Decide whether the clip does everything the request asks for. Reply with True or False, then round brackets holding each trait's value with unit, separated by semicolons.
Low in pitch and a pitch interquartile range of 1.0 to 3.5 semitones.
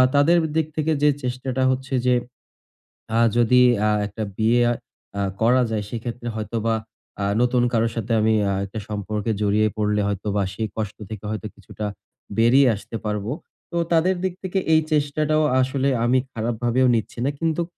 False (120 Hz; 4.0 semitones)